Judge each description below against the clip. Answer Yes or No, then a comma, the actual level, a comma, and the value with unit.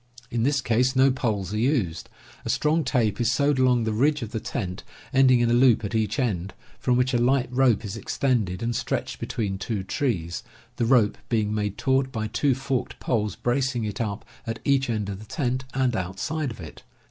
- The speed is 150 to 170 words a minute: No, fast, 205 wpm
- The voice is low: Yes, low, 120 Hz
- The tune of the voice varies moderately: Yes, average, 3.7 semitones